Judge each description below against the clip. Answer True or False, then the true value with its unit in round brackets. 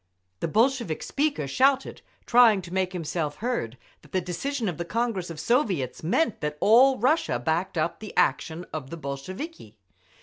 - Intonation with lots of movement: True (7.6 semitones)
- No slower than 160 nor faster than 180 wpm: True (165 wpm)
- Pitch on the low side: False (185 Hz)